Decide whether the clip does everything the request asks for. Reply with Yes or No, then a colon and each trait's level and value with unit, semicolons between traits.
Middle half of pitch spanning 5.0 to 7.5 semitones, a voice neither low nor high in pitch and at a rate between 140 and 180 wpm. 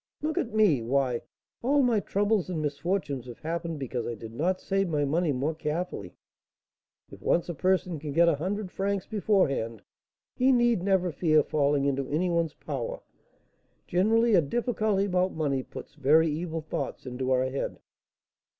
Yes: wide, 5.6 semitones; medium, 165 Hz; average, 165 wpm